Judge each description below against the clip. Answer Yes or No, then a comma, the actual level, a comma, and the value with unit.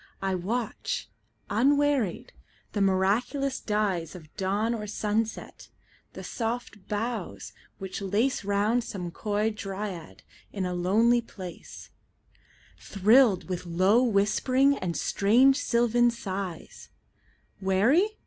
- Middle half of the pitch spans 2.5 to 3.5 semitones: No, average, 3.9 semitones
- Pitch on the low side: No, high, 210 Hz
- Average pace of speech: No, slow, 90 wpm